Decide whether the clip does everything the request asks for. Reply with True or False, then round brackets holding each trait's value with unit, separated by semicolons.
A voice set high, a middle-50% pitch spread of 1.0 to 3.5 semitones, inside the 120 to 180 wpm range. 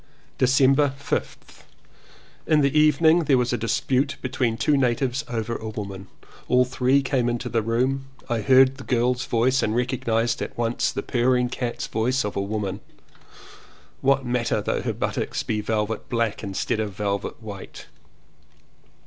False (120 Hz; 3.0 semitones; 160 wpm)